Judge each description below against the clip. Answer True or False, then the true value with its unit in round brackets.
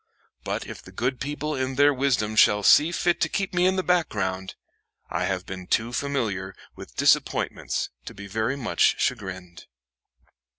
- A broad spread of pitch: True (7.0 semitones)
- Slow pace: False (165 wpm)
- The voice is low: True (120 Hz)